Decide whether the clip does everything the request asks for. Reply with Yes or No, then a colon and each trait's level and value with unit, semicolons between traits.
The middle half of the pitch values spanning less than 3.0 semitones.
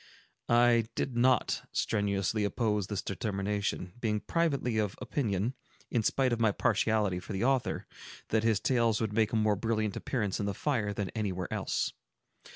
Yes: narrow, 2.5 semitones